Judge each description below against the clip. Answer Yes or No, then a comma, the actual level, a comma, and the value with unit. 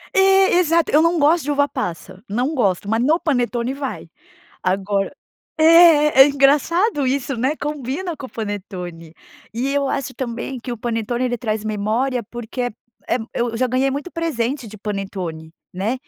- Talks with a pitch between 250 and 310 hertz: Yes, very high, 255 Hz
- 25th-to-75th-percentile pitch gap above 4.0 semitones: Yes, average, 5.2 semitones